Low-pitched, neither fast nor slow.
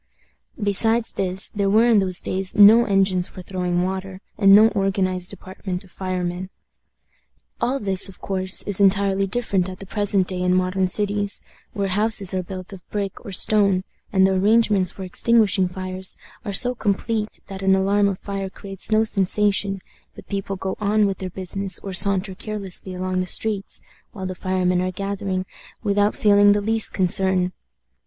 No: high, 195 Hz; average, 170 wpm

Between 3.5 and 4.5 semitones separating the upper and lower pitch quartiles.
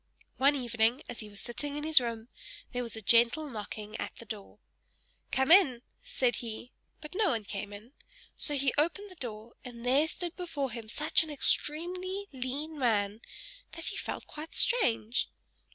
No: wide, 5.4 semitones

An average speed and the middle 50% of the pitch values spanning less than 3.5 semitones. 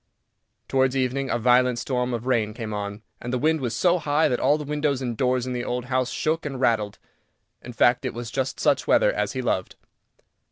No: fast, 215 wpm; narrow, 2.4 semitones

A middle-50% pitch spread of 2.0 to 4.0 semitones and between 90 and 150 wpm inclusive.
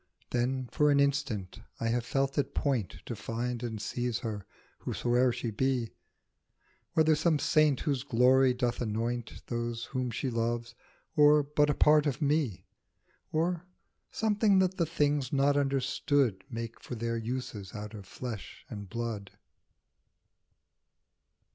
Yes: average, 3.7 semitones; average, 140 wpm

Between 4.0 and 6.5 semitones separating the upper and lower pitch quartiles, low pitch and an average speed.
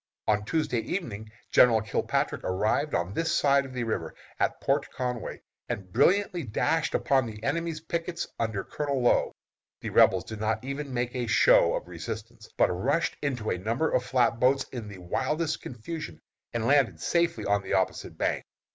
Yes: average, 5.0 semitones; low, 125 Hz; average, 170 wpm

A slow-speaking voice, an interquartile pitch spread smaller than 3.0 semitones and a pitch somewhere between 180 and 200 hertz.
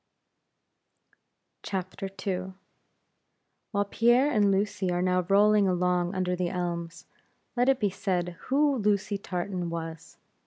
Yes: slow, 115 wpm; narrow, 2.5 semitones; high, 190 Hz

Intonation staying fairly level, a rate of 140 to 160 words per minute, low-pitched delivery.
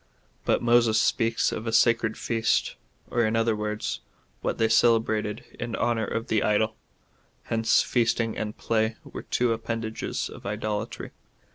Yes: narrow, 1.0 semitones; average, 150 wpm; low, 115 Hz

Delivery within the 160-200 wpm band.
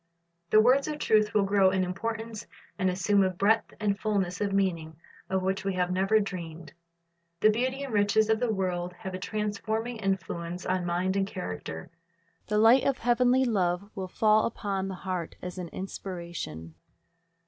Yes: average, 170 wpm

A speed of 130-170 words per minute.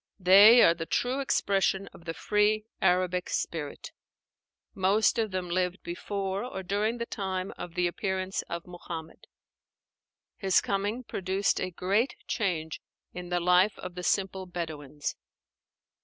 Yes: average, 140 wpm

